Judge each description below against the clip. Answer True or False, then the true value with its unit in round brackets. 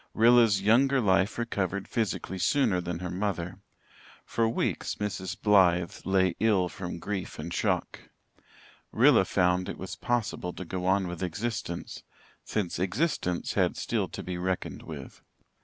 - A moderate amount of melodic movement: True (3.4 semitones)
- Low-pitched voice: True (95 Hz)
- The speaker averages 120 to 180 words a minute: True (140 wpm)